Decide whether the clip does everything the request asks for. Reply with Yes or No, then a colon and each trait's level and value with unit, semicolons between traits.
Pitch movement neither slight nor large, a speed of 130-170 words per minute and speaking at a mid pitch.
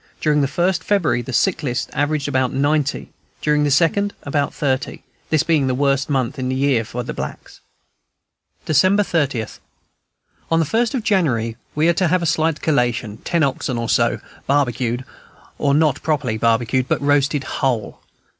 Yes: average, 3.7 semitones; average, 165 wpm; medium, 145 Hz